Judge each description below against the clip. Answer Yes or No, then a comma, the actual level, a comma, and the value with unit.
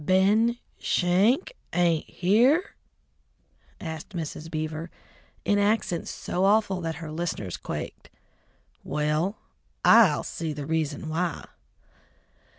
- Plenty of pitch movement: No, average, 4.4 semitones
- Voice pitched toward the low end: No, medium, 175 Hz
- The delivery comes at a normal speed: No, slow, 100 wpm